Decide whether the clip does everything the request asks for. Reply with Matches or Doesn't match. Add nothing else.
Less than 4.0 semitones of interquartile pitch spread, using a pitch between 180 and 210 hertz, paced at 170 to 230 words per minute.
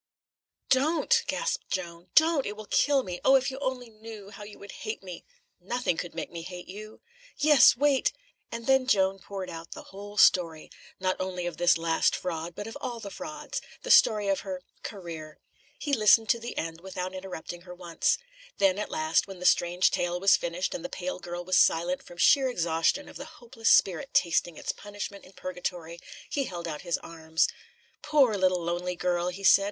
Doesn't match